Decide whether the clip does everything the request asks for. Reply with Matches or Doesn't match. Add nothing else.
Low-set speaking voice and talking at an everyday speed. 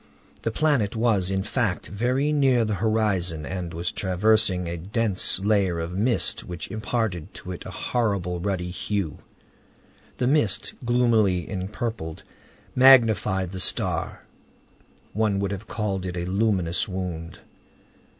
Doesn't match